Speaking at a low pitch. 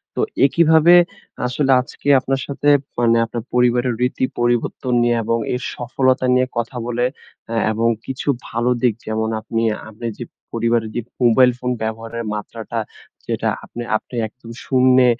Yes: low, 120 Hz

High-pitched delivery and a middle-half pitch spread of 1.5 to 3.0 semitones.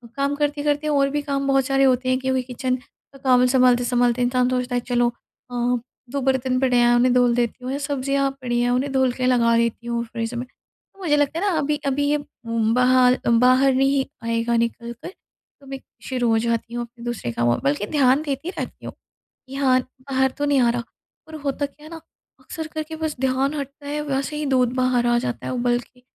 Yes: very high, 255 Hz; narrow, 2.5 semitones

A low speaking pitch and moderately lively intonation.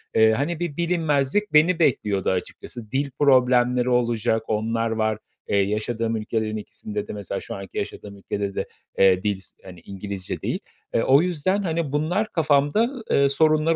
No: low, 125 Hz; wide, 6.4 semitones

